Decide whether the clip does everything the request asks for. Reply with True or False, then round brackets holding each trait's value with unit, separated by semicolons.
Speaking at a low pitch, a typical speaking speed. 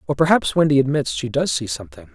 False (125 Hz; 225 wpm)